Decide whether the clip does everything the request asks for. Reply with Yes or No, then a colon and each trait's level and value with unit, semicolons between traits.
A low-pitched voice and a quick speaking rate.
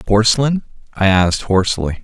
No: low, 105 Hz; slow, 120 wpm